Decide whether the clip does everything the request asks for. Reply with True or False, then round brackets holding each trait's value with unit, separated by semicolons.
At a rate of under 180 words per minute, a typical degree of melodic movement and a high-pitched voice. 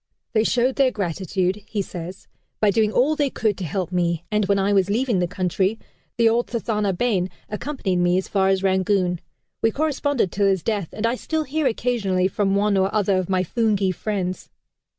False (195 wpm; 3.5 semitones; 200 Hz)